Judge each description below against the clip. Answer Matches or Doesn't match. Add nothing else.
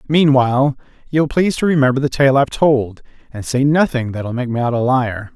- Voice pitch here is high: Doesn't match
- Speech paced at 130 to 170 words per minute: Doesn't match